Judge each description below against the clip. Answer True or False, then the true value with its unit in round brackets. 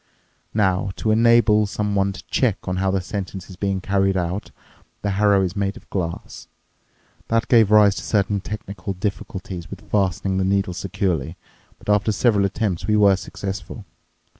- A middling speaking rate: True (165 wpm)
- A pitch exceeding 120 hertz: False (100 Hz)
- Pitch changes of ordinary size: False (1.8 semitones)